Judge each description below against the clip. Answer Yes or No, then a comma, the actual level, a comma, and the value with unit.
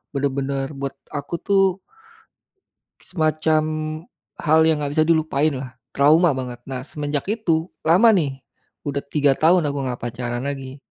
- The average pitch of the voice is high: No, medium, 145 Hz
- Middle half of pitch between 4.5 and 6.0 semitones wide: No, average, 2.8 semitones